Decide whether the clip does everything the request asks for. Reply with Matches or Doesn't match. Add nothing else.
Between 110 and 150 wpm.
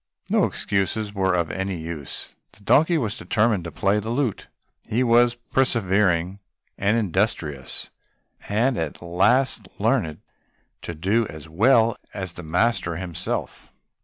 Matches